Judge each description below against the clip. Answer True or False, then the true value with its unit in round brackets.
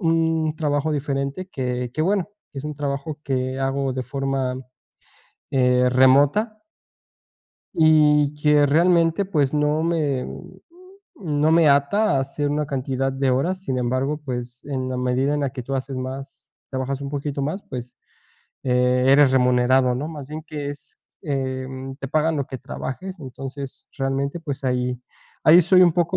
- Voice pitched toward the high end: False (140 Hz)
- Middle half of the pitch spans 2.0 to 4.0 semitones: True (2.7 semitones)